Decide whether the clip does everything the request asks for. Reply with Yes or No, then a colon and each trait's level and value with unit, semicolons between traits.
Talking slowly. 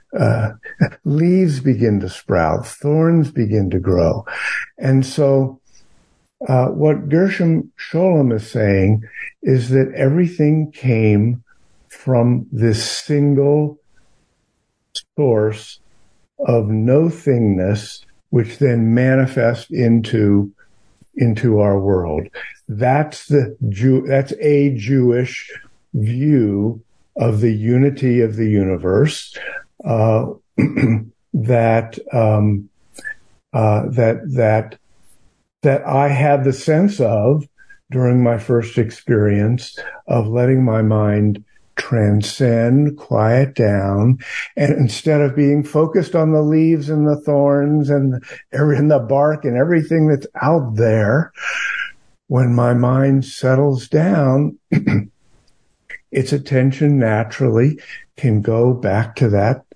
Yes: slow, 105 wpm